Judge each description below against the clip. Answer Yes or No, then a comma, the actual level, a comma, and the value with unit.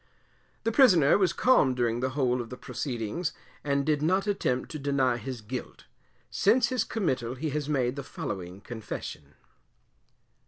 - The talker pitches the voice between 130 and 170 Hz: Yes, low, 135 Hz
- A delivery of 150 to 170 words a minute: Yes, average, 155 wpm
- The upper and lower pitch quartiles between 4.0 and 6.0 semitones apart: Yes, average, 5.0 semitones